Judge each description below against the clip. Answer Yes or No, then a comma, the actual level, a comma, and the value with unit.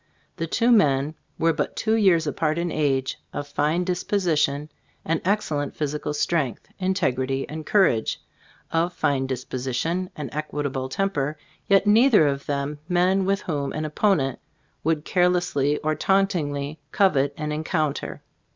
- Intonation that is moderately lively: Yes, average, 4.2 semitones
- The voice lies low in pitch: No, medium, 155 Hz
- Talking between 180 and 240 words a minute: No, average, 140 wpm